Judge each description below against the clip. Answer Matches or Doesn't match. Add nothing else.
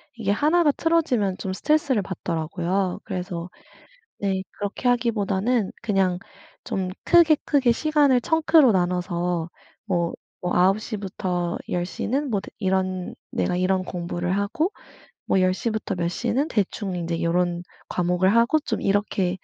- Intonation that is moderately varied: Matches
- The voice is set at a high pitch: Matches